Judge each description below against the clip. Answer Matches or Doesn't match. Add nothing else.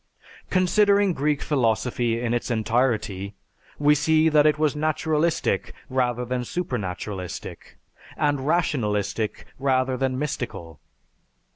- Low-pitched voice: Matches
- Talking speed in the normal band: Doesn't match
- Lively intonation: Doesn't match